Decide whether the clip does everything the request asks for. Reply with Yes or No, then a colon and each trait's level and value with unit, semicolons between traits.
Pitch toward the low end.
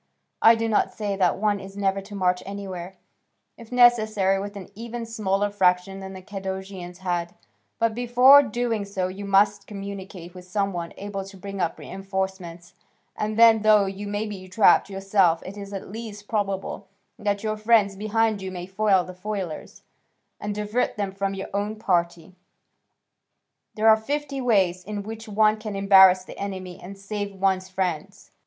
No: high, 200 Hz